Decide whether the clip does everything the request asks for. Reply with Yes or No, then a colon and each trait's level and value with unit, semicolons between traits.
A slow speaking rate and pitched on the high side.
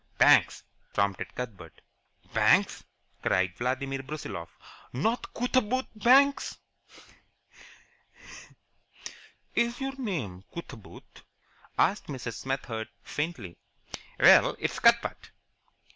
No: slow, 80 wpm; low, 135 Hz